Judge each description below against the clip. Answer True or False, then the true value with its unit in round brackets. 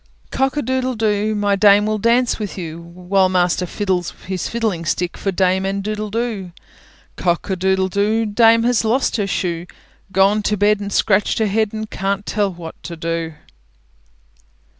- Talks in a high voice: True (200 Hz)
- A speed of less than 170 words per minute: False (175 wpm)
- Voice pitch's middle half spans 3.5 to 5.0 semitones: False (2.9 semitones)